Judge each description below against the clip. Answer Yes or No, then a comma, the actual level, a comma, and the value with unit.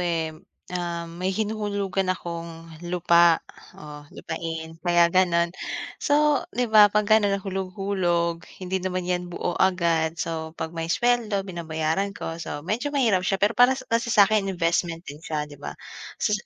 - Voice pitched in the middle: Yes, medium, 180 Hz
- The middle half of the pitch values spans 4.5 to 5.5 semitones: No, average, 3.3 semitones